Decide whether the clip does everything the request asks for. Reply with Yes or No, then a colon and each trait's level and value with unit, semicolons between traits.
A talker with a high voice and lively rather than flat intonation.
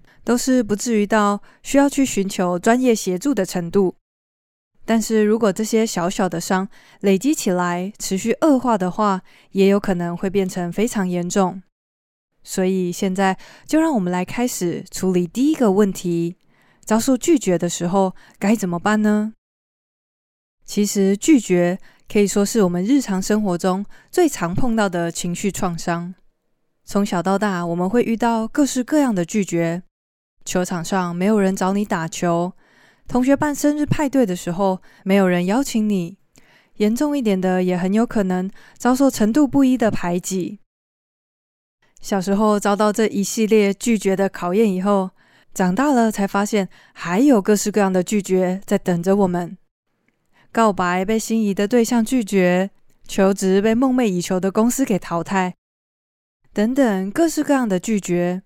No: high, 200 Hz; average, 3.6 semitones